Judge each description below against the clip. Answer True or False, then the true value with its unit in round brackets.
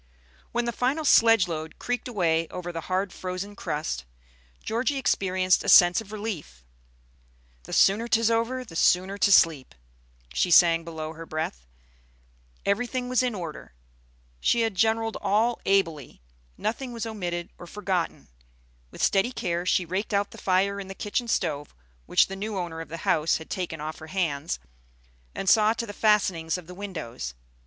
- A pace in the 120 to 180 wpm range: True (165 wpm)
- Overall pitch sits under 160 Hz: False (190 Hz)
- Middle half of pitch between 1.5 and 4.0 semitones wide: False (5.0 semitones)